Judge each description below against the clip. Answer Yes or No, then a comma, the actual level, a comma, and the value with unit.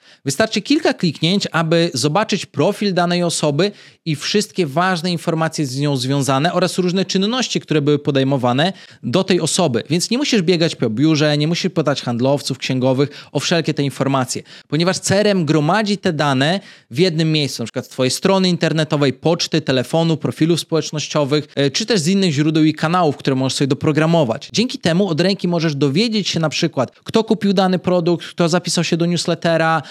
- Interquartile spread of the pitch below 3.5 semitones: No, average, 4.0 semitones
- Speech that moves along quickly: Yes, fast, 175 wpm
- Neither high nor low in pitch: Yes, medium, 165 Hz